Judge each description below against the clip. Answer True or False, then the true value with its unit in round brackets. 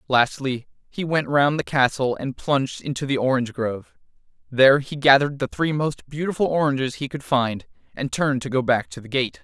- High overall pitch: False (135 Hz)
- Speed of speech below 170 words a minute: False (195 wpm)